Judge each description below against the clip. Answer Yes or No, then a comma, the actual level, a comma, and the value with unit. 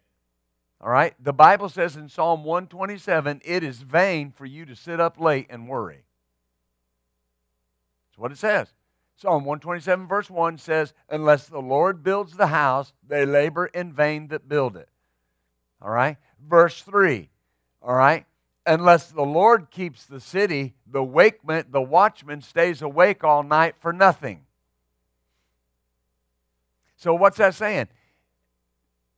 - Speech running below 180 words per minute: Yes, average, 140 wpm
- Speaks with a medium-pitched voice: Yes, medium, 145 Hz